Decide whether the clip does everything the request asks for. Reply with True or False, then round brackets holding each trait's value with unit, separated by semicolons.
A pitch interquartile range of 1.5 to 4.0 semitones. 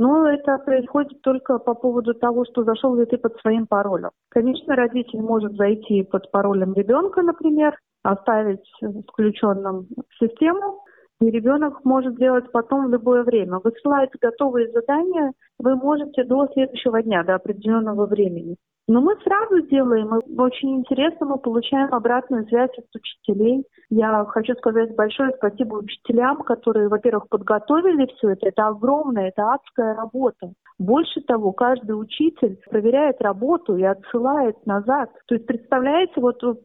True (3.7 semitones)